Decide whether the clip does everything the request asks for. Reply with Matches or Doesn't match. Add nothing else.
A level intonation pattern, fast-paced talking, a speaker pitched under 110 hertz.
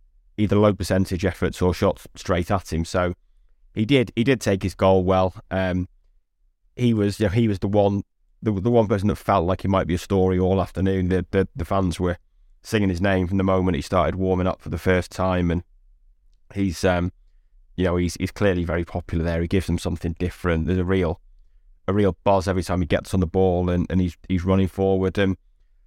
Matches